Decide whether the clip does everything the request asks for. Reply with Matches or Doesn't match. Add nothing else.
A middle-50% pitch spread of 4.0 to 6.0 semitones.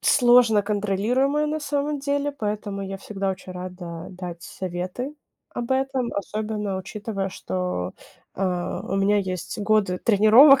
Matches